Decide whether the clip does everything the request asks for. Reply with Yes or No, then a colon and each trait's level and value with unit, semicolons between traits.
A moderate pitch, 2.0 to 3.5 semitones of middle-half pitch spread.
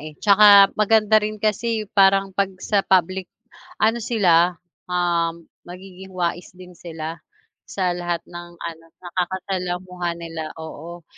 Yes: medium, 180 Hz; narrow, 2.5 semitones